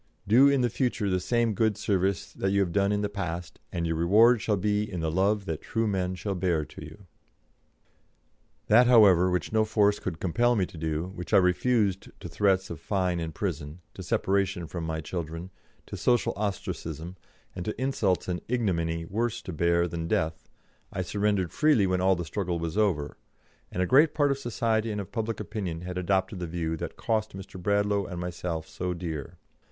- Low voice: Yes, very low, 95 Hz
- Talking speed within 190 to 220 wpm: Yes, average, 200 wpm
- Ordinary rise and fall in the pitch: Yes, average, 3.6 semitones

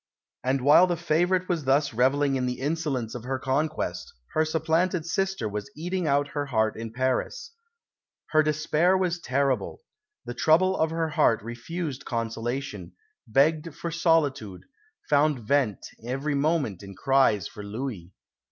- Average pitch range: Yes, average, 4.9 semitones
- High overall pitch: No, medium, 140 Hz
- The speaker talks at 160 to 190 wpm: No, average, 145 wpm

